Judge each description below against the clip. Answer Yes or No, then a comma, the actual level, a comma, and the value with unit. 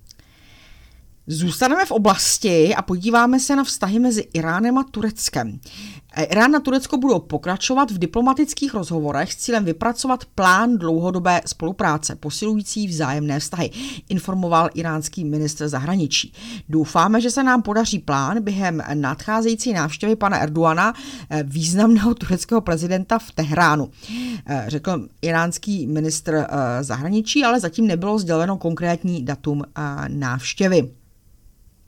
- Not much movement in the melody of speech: No, wide, 6.8 semitones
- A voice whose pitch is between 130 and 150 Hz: No, medium, 175 Hz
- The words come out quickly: No, slow, 115 wpm